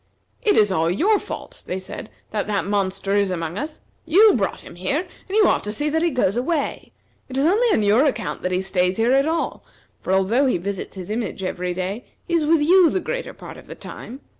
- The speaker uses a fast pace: Yes, fast, 235 wpm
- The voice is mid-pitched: No, high, 225 Hz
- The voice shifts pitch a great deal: Yes, wide, 8.9 semitones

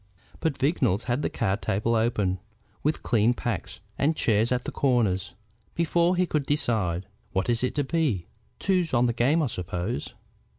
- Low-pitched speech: Yes, low, 120 Hz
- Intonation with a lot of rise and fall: Yes, wide, 6.0 semitones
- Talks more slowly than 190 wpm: Yes, average, 170 wpm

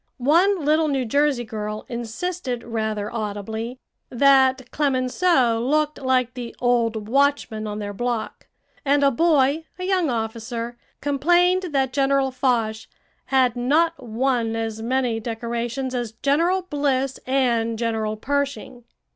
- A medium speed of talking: No, slow, 125 wpm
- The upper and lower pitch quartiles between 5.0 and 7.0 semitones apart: No, average, 3.7 semitones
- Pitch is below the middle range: No, very high, 255 Hz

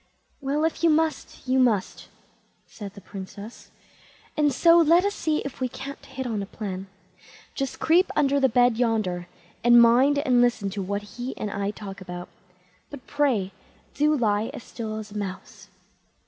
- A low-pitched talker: No, high, 240 Hz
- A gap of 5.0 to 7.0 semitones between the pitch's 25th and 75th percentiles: Yes, wide, 5.6 semitones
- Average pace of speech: Yes, average, 175 wpm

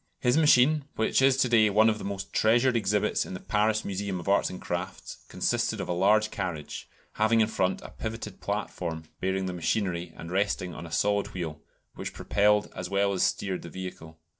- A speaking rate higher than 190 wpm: Yes, average, 200 wpm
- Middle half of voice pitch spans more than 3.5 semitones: No, average, 3.1 semitones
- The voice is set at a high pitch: No, low, 100 Hz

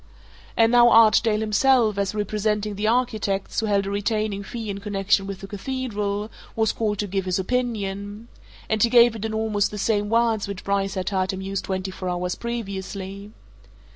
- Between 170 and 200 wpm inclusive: Yes, average, 185 wpm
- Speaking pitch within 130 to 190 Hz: No, high, 205 Hz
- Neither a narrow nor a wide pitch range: No, narrow, 2.2 semitones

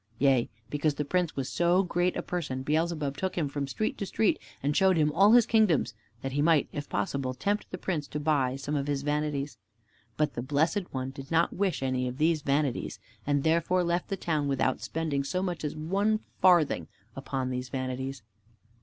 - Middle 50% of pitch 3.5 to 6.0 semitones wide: Yes, average, 4.2 semitones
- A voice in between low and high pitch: Yes, medium, 150 Hz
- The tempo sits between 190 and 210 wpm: Yes, average, 200 wpm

